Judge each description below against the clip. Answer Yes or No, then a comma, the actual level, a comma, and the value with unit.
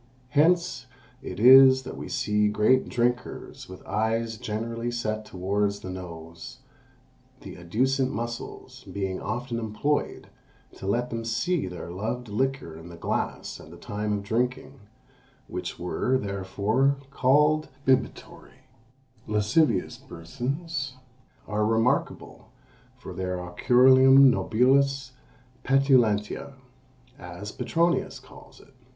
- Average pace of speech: No, slow, 110 wpm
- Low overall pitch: Yes, low, 115 Hz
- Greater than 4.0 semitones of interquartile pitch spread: Yes, average, 4.5 semitones